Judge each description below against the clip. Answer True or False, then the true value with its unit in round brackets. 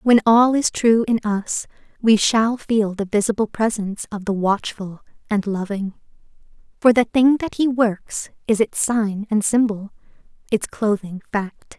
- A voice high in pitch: True (215 Hz)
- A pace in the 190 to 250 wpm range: False (160 wpm)